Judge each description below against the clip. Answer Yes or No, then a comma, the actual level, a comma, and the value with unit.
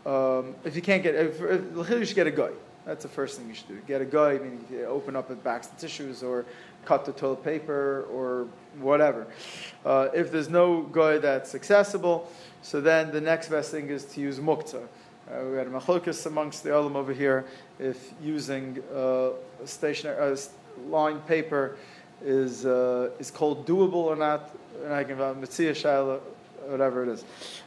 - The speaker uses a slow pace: No, average, 185 wpm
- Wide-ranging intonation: No, average, 3.2 semitones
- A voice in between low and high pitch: Yes, medium, 145 Hz